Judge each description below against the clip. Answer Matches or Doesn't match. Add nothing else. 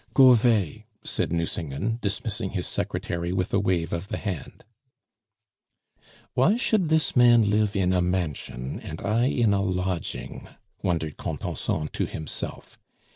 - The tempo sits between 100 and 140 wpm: Matches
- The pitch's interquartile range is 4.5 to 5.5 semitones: Matches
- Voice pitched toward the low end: Matches